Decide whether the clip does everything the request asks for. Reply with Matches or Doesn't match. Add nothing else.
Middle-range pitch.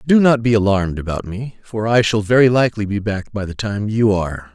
Doesn't match